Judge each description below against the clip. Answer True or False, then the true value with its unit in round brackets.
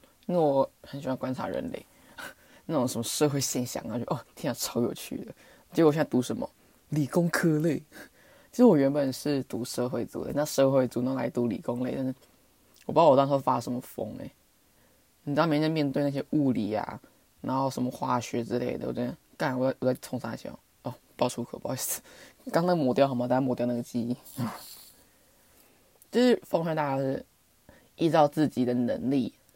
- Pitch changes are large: False (3.3 semitones)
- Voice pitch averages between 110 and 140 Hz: True (135 Hz)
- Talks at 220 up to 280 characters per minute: False (295 characters per minute)